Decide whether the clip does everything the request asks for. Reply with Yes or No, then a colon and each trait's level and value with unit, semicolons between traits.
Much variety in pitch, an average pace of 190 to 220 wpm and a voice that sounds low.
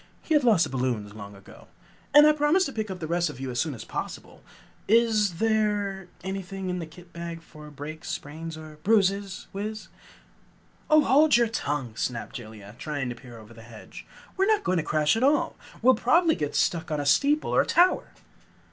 No: wide, 7.6 semitones; average, 200 wpm; medium, 175 Hz